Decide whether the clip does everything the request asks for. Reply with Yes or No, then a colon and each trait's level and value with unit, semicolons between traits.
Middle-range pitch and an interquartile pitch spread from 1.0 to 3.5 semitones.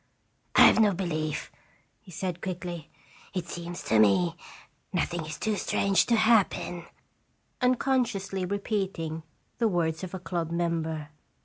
Yes: medium, 175 Hz; average, 3.2 semitones